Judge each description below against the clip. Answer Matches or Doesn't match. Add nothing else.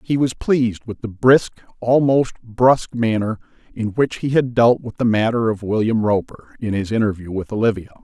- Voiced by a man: Matches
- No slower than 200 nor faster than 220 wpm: Doesn't match